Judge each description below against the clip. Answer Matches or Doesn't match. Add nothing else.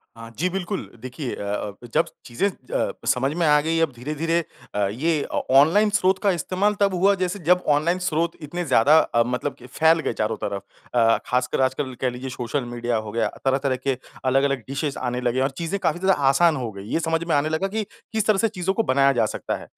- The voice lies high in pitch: Doesn't match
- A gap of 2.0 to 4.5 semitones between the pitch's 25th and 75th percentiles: Doesn't match